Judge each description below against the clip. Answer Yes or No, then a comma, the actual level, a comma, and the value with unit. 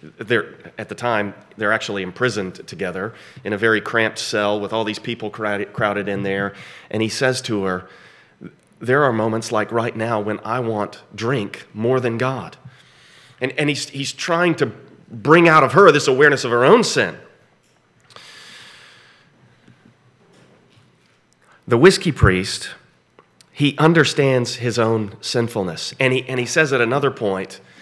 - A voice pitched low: Yes, low, 115 Hz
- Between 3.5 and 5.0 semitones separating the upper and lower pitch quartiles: Yes, average, 3.9 semitones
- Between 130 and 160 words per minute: Yes, average, 150 wpm